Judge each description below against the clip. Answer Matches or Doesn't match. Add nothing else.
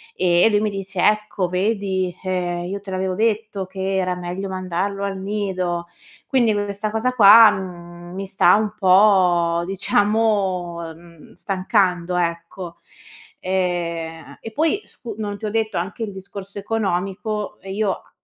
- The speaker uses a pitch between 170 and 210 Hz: Matches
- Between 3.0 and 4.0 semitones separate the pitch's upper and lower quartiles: Doesn't match